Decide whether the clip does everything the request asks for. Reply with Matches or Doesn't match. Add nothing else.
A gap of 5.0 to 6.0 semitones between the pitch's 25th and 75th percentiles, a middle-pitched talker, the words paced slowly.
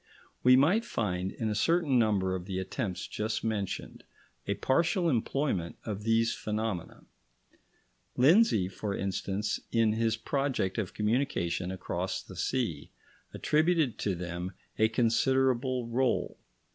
Doesn't match